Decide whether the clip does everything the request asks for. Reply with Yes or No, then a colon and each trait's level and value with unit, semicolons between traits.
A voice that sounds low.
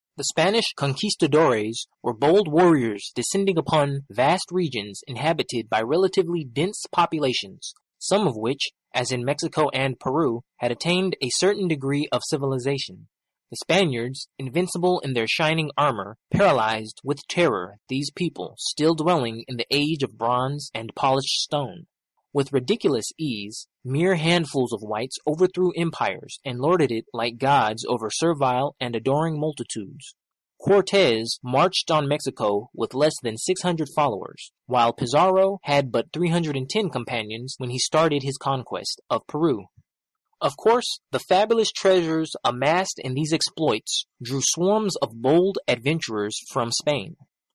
No: medium, 145 Hz